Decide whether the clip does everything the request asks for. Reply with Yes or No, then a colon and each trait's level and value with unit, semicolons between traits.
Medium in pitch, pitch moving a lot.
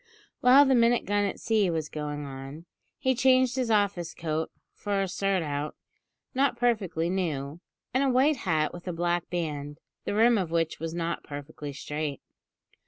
Yes: medium, 175 Hz; wide, 7.1 semitones